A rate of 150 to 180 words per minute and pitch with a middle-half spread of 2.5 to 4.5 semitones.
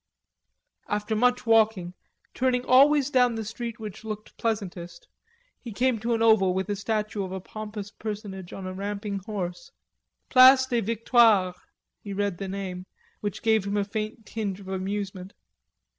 Yes: average, 160 wpm; average, 2.8 semitones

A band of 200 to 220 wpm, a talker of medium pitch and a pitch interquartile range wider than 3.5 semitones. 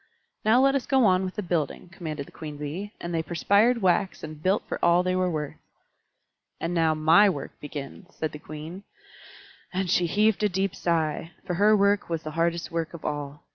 Yes: fast, 205 wpm; medium, 170 Hz; average, 3.9 semitones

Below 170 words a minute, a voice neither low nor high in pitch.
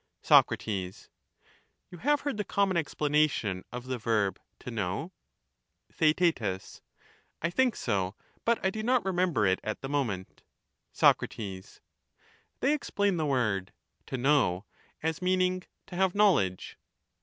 Yes: slow, 135 wpm; medium, 145 Hz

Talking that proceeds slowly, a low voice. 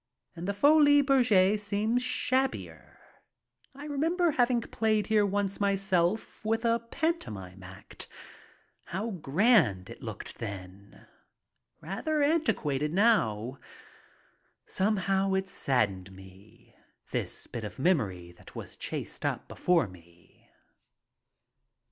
No: slow, 110 wpm; high, 195 Hz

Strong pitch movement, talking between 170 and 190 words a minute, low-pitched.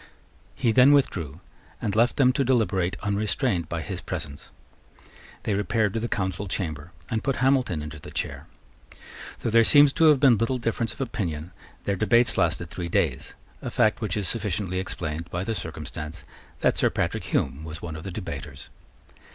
Yes: wide, 5.8 semitones; average, 175 wpm; low, 100 Hz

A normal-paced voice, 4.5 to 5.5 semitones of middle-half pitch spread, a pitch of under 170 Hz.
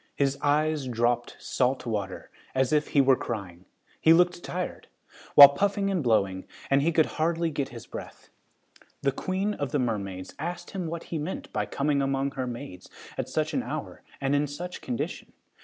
Yes: average, 180 wpm; average, 5.0 semitones; medium, 140 Hz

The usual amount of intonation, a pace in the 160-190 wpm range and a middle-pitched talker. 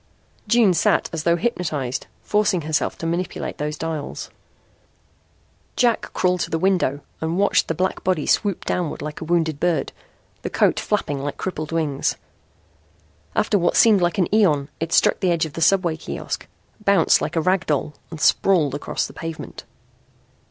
Yes: average, 3.3 semitones; average, 165 wpm; medium, 165 Hz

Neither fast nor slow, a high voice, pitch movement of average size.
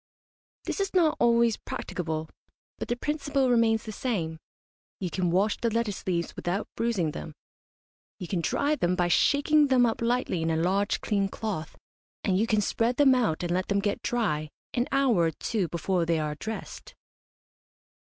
No: average, 175 wpm; high, 205 Hz; wide, 5.7 semitones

